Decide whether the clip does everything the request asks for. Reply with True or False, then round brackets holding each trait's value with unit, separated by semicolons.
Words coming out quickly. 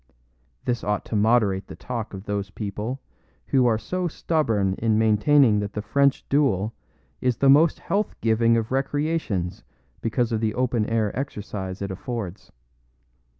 False (150 wpm)